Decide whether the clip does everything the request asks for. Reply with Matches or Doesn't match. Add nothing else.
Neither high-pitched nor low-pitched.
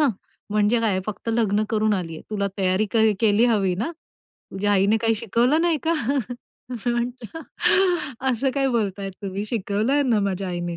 Doesn't match